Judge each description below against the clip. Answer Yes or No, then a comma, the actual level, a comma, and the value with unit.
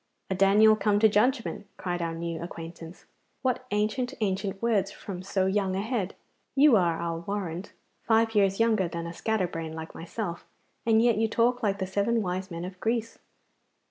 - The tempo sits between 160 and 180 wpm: Yes, average, 175 wpm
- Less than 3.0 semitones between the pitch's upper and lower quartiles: No, average, 3.9 semitones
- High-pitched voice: Yes, high, 200 Hz